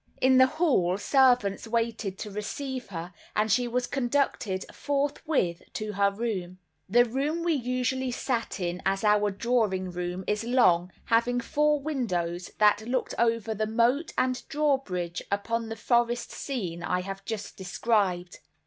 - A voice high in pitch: Yes, high, 230 Hz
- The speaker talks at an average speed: Yes, average, 150 wpm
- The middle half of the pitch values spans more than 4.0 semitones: Yes, average, 4.7 semitones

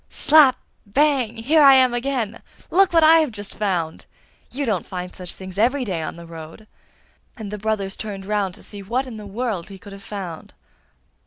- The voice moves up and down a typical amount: Yes, average, 5.0 semitones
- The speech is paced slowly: No, average, 195 wpm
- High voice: Yes, high, 215 Hz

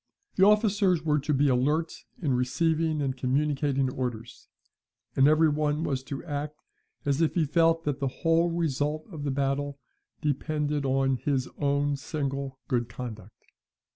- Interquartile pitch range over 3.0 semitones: No, average, 2.7 semitones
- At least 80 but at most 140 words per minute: No, average, 150 wpm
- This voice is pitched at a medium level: Yes, medium, 145 Hz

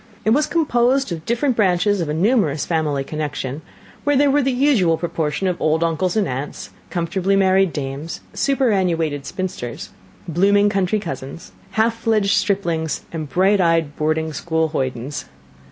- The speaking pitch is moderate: Yes, medium, 175 Hz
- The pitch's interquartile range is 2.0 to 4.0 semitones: No, average, 5.1 semitones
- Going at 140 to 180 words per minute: Yes, average, 150 wpm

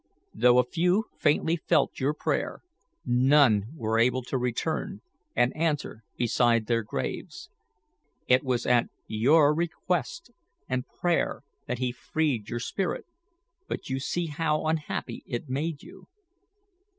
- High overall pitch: No, low, 130 Hz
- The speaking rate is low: Yes, slow, 130 wpm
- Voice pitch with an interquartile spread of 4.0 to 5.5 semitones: Yes, average, 4.6 semitones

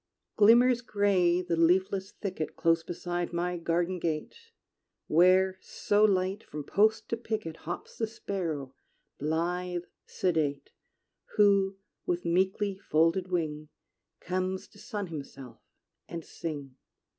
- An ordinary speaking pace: No, slow, 115 wpm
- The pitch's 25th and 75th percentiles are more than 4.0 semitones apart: No, average, 2.9 semitones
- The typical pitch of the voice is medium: Yes, medium, 180 Hz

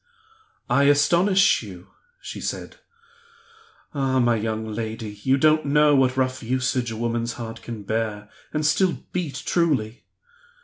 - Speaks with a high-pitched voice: No, low, 130 Hz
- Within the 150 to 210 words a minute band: No, slow, 135 wpm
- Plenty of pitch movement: No, average, 4.5 semitones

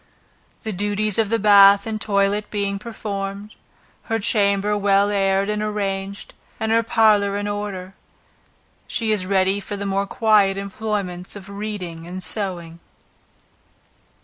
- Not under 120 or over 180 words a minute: Yes, slow, 135 wpm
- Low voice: No, high, 200 Hz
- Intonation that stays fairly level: Yes, narrow, 1.4 semitones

